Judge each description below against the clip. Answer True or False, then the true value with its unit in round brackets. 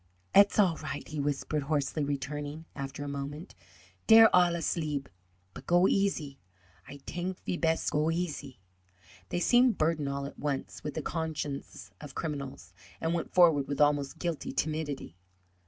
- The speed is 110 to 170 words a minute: True (155 wpm)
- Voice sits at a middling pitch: True (150 Hz)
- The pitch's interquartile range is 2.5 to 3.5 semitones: True (3.1 semitones)